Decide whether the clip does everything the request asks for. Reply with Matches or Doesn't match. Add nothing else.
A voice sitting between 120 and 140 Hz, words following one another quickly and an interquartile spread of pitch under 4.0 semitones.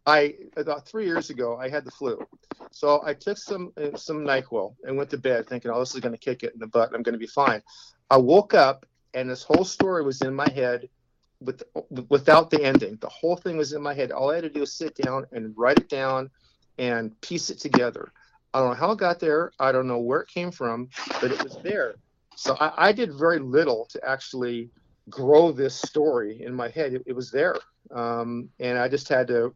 Matches